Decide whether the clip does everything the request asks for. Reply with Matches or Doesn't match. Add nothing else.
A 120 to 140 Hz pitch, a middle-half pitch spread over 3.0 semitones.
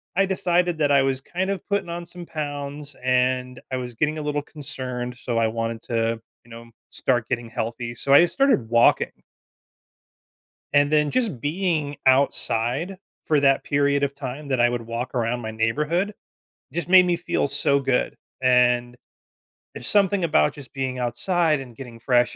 Matches